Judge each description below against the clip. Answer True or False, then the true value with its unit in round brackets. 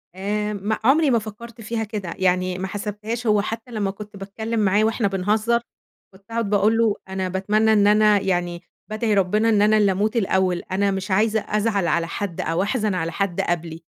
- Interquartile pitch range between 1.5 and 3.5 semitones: True (2.5 semitones)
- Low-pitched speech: False (205 Hz)